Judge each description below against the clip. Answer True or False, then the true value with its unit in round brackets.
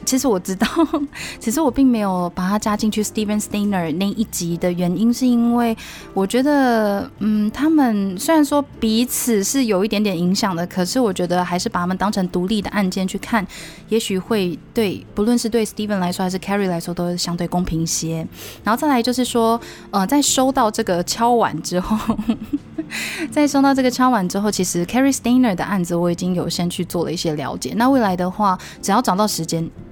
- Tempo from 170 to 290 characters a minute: False (360 characters per minute)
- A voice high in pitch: True (210 Hz)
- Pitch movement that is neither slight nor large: True (4.8 semitones)